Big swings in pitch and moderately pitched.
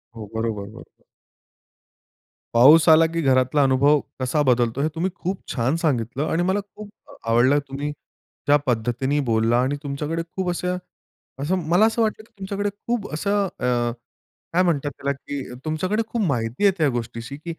Yes: wide, 6.1 semitones; medium, 145 Hz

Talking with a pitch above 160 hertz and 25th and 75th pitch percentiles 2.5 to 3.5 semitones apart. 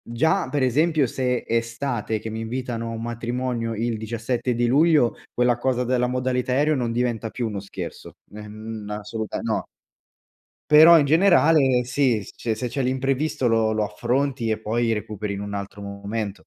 No: low, 120 Hz; average, 2.8 semitones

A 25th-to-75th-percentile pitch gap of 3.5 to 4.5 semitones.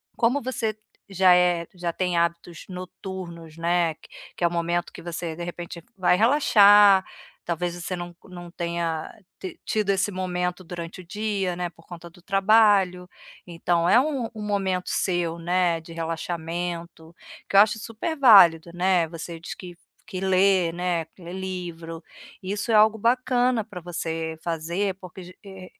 No: narrow, 2.6 semitones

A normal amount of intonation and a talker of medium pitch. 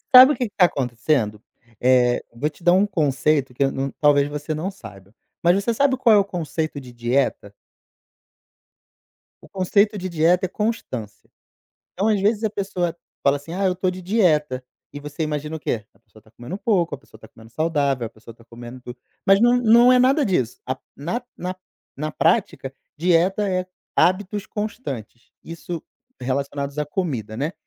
No: wide, 6.9 semitones; medium, 160 Hz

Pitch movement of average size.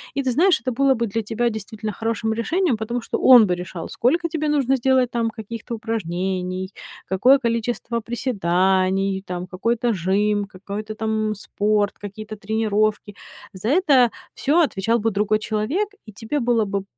Yes: average, 3.1 semitones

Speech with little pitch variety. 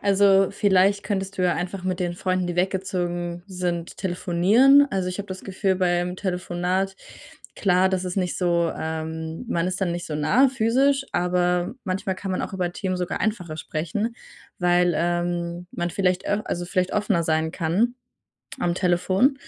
Yes: narrow, 1.8 semitones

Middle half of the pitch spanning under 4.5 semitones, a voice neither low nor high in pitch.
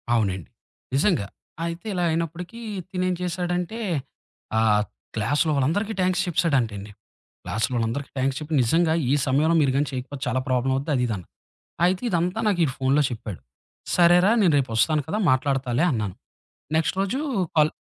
No: wide, 5.6 semitones; medium, 150 Hz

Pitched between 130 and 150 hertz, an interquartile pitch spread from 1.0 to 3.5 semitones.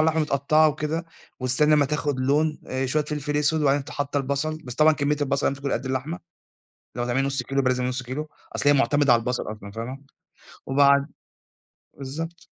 Yes: medium, 140 Hz; narrow, 2.5 semitones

